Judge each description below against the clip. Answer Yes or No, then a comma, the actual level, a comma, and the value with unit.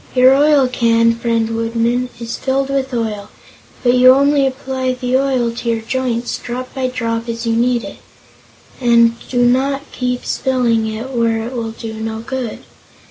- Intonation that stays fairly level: Yes, narrow, 2.2 semitones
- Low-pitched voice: No, high, 245 Hz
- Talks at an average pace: Yes, average, 170 wpm